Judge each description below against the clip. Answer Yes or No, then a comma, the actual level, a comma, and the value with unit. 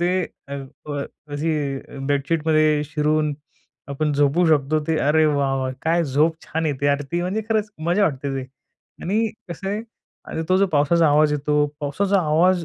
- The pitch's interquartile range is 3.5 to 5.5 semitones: No, average, 2.9 semitones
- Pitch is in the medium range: Yes, medium, 155 Hz